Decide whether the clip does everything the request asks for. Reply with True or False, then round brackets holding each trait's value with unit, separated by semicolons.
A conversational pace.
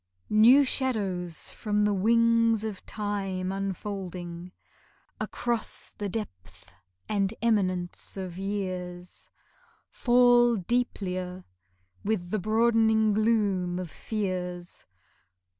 False (90 wpm)